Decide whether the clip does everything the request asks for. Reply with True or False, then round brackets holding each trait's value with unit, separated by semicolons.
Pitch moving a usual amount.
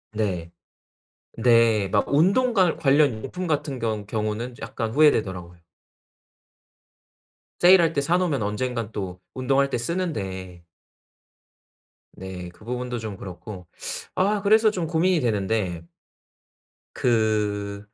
False (7.3 semitones)